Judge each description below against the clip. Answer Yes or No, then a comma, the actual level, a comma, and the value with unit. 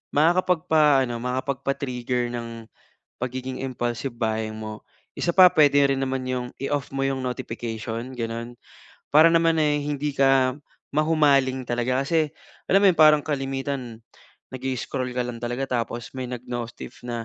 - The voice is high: No, low, 130 Hz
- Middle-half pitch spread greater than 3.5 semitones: No, average, 3.0 semitones